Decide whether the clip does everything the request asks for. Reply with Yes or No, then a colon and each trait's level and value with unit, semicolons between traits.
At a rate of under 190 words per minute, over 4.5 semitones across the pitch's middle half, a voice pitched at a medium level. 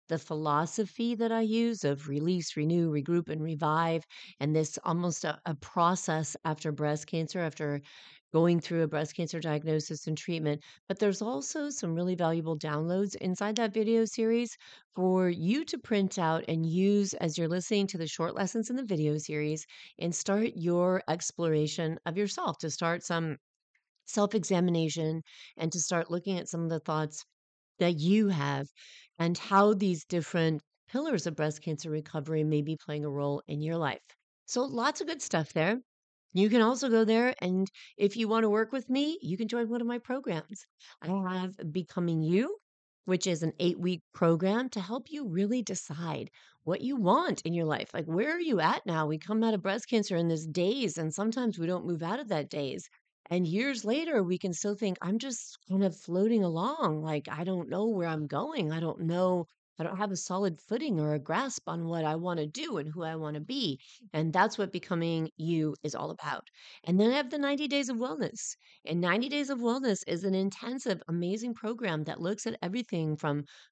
No: average, 200 wpm; average, 5.0 semitones; medium, 175 Hz